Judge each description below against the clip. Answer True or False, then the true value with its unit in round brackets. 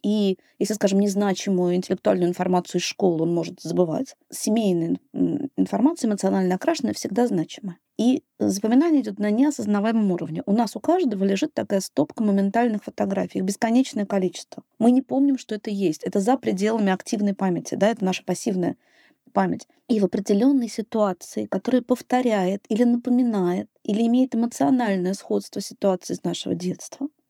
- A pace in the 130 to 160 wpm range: True (145 wpm)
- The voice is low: False (210 Hz)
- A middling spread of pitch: True (4.4 semitones)